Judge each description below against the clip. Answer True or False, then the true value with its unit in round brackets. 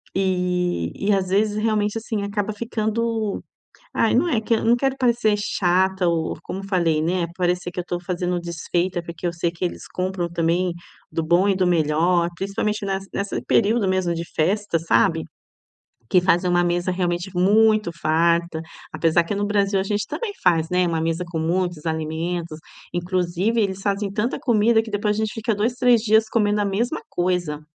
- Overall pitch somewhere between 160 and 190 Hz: True (185 Hz)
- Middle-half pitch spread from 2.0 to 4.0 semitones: True (3.3 semitones)